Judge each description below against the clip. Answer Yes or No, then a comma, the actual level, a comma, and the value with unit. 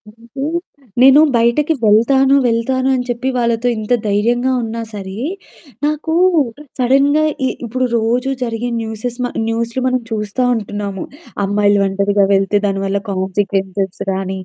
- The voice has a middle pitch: No, high, 230 Hz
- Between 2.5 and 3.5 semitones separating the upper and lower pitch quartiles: No, average, 3.9 semitones